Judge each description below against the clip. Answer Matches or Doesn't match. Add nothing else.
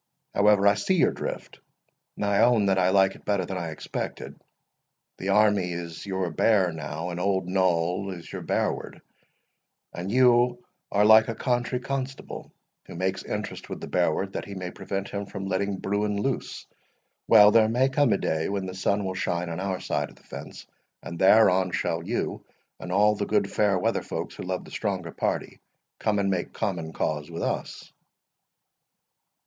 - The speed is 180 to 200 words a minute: Matches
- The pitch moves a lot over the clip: Doesn't match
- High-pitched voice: Doesn't match